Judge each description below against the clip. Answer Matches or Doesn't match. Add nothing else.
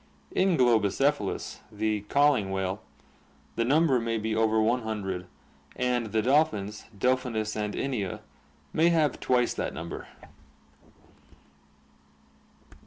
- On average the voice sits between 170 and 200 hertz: Doesn't match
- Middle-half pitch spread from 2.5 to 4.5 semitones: Matches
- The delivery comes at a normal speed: Doesn't match